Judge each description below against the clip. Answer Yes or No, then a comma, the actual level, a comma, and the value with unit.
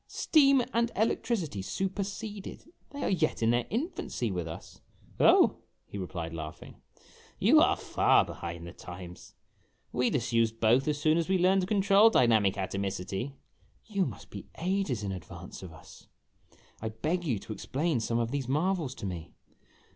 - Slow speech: No, average, 165 wpm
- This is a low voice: Yes, low, 125 Hz